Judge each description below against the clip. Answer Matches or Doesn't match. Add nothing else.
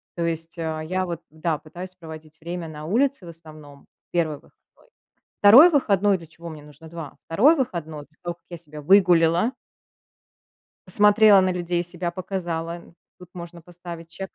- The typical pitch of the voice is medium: Matches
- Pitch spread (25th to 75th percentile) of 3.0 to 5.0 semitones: Doesn't match